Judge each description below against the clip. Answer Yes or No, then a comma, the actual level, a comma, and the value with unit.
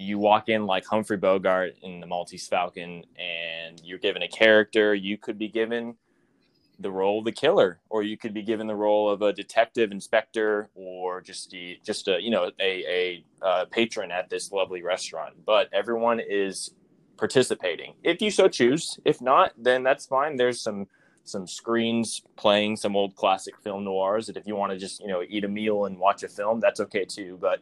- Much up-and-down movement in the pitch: No, average, 3.1 semitones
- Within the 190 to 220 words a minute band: Yes, average, 200 wpm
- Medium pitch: No, low, 105 Hz